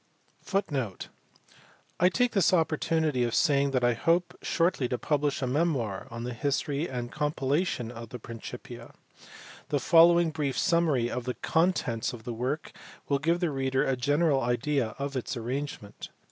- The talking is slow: No, average, 160 wpm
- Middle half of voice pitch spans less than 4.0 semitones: No, average, 4.7 semitones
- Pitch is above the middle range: No, medium, 140 Hz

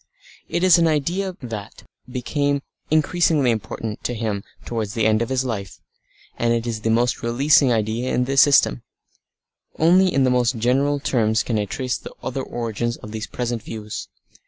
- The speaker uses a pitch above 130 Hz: No, low, 120 Hz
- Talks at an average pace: Yes, average, 175 wpm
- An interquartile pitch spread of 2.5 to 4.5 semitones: Yes, average, 4.0 semitones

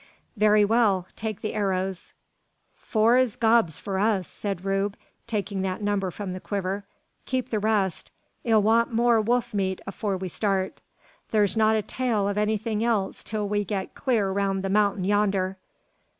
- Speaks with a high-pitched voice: Yes, high, 205 Hz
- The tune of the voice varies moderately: No, narrow, 2.2 semitones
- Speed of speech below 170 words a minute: Yes, average, 160 wpm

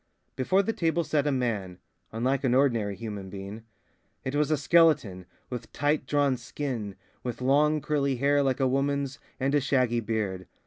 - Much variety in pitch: No, average, 4.1 semitones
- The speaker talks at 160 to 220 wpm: Yes, average, 170 wpm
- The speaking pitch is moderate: No, low, 130 Hz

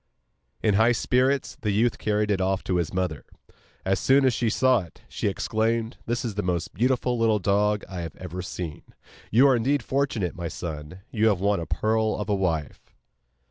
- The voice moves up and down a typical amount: Yes, average, 4.2 semitones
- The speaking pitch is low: Yes, low, 105 Hz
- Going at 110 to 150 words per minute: No, average, 195 wpm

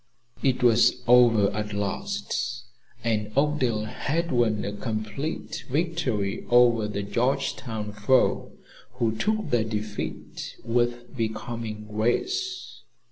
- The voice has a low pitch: Yes, low, 115 Hz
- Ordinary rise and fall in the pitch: Yes, average, 3.5 semitones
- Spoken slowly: Yes, slow, 105 wpm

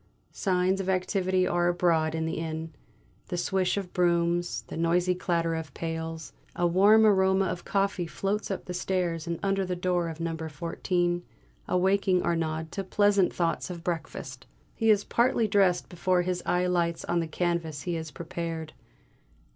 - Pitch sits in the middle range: Yes, medium, 175 Hz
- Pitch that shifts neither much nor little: No, narrow, 2.2 semitones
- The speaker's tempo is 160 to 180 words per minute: Yes, average, 165 wpm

